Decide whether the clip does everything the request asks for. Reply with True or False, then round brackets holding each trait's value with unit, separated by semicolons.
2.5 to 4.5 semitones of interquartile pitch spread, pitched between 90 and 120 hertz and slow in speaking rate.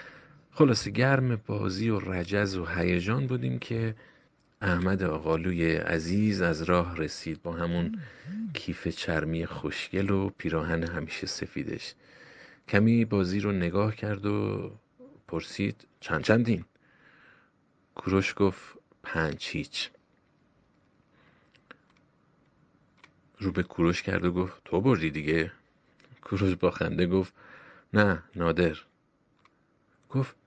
True (4.2 semitones; 95 Hz; 100 wpm)